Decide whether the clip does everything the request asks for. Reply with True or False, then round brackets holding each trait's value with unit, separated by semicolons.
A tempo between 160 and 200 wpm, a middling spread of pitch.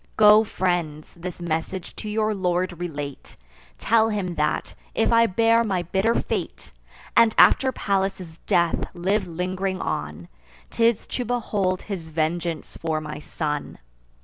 False (135 wpm; 4.4 semitones)